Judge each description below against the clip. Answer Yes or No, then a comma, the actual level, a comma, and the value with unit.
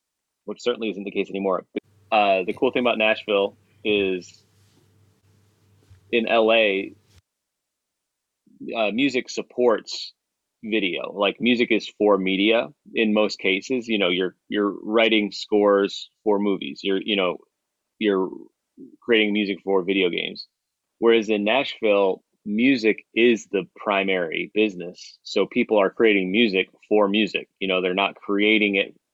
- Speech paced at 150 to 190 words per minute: No, slow, 135 wpm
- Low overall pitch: Yes, low, 105 Hz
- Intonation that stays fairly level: Yes, narrow, 2.1 semitones